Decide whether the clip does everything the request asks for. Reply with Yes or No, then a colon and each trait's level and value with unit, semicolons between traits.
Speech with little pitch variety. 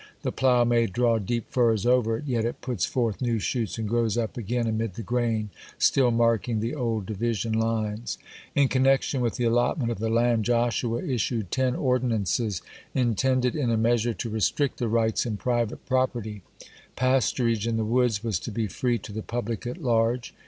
Yes: narrow, 1.8 semitones